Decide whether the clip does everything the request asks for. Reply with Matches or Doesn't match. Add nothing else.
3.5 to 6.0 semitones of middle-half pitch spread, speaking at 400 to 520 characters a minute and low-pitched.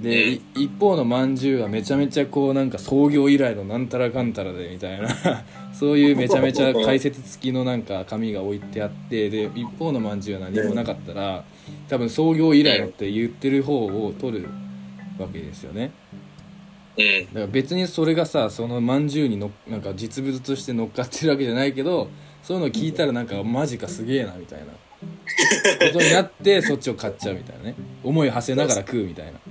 Matches